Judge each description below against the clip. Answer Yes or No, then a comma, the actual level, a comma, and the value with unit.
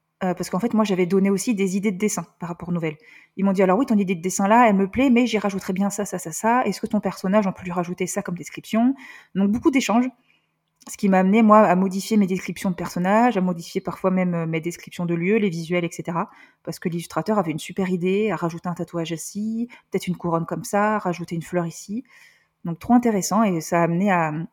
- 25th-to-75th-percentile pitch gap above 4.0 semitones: No, average, 3.4 semitones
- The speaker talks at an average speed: No, fast, 250 wpm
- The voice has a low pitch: No, high, 190 Hz